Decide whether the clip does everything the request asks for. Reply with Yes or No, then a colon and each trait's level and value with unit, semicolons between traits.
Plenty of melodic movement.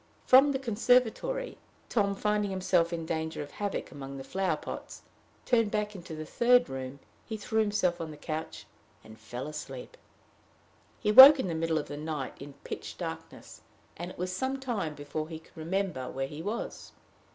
Yes: wide, 5.8 semitones